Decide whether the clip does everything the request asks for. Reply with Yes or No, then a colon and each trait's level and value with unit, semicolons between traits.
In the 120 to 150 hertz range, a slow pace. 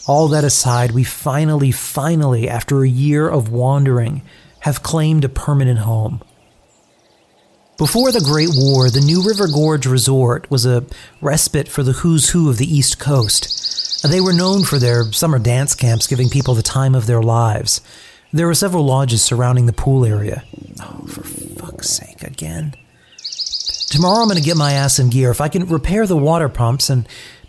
No: low, 135 Hz; average, 175 wpm